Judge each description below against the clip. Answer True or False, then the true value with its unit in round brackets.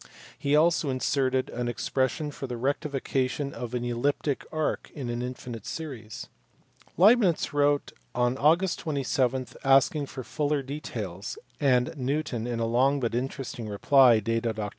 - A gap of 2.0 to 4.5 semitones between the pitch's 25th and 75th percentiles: True (3.0 semitones)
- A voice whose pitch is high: False (135 Hz)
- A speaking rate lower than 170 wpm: True (140 wpm)